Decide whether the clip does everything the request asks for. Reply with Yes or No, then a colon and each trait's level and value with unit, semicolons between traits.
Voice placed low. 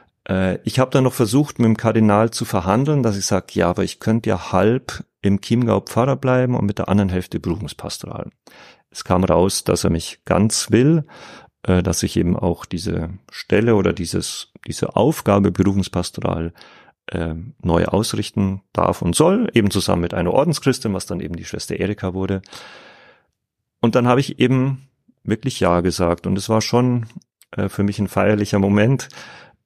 Yes: low, 105 Hz